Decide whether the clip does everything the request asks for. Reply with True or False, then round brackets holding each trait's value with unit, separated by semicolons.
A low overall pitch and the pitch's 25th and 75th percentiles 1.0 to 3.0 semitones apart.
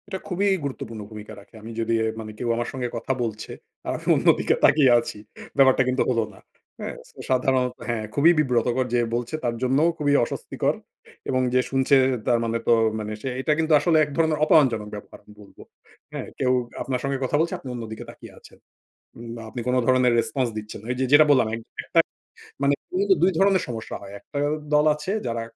False (130 Hz; 3.7 semitones)